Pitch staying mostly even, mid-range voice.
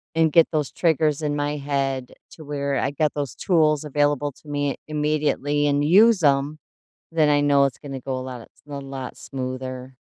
Yes: narrow, 1.8 semitones; medium, 145 Hz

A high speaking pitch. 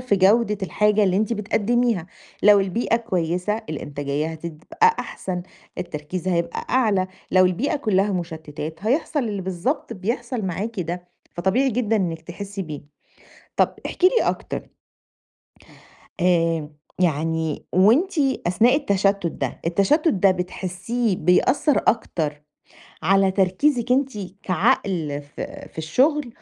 Yes: high, 195 Hz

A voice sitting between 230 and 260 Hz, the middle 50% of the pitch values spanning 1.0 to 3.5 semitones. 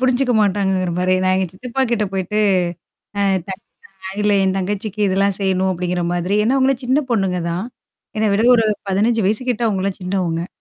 No: high, 195 Hz; average, 3.0 semitones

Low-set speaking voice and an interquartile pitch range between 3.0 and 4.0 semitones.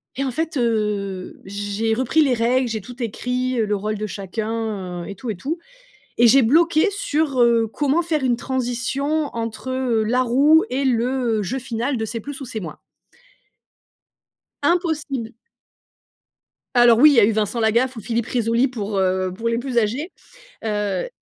No: high, 235 Hz; average, 3.5 semitones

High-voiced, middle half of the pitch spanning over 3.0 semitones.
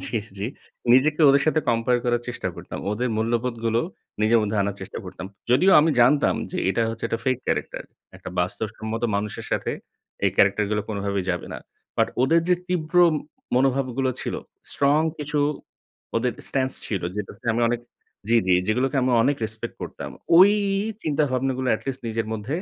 No: low, 120 Hz; average, 3.8 semitones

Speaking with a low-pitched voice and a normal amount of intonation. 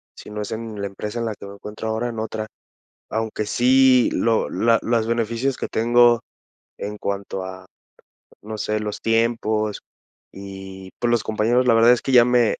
No: low, 110 Hz; narrow, 2.1 semitones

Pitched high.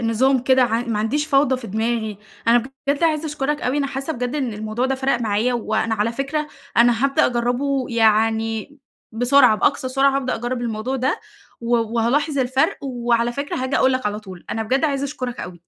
Yes: high, 245 Hz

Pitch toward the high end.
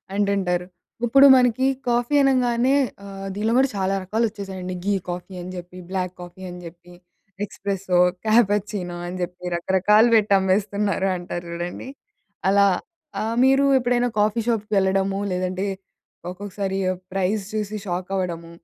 Yes: high, 195 Hz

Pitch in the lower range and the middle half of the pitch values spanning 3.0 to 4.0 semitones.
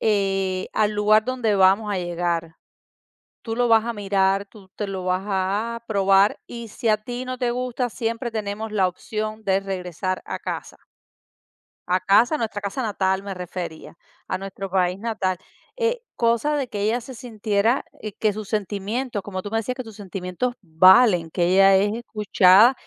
No: high, 205 Hz; average, 3.3 semitones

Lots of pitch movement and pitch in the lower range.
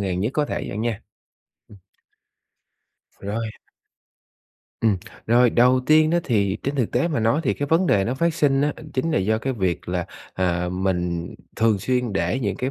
Yes: wide, 5.8 semitones; low, 115 Hz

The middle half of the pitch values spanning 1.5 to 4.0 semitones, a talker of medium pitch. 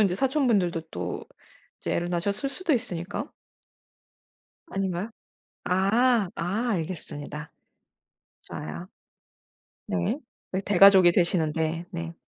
Yes: average, 3.5 semitones; medium, 180 Hz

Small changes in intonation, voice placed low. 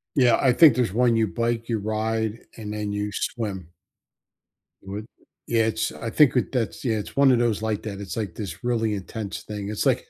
Yes: narrow, 2.3 semitones; low, 110 Hz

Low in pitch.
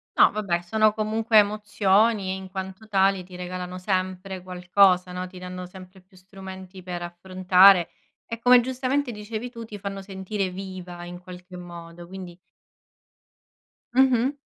No: high, 190 Hz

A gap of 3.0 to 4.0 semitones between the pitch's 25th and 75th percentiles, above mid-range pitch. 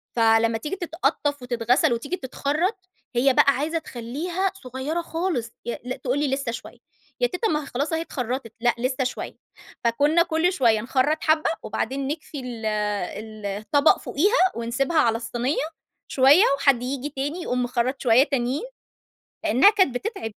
No: average, 4.8 semitones; very high, 270 Hz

